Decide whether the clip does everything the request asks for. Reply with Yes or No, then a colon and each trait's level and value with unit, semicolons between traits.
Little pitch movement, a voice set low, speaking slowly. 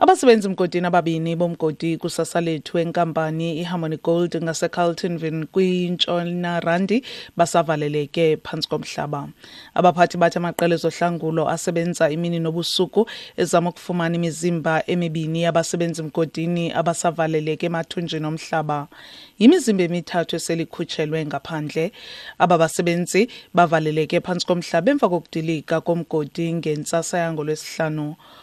No: narrow, 1.6 semitones; medium, 170 Hz; slow, 90 wpm